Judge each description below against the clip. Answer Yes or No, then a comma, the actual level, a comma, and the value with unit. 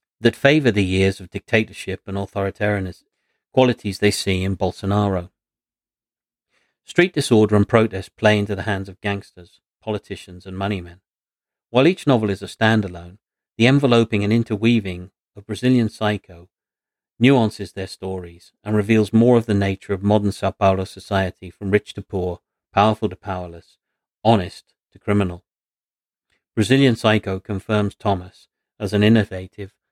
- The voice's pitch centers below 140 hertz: Yes, low, 100 Hz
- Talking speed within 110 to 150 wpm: Yes, average, 140 wpm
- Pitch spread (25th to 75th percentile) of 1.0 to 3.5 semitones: Yes, narrow, 2.5 semitones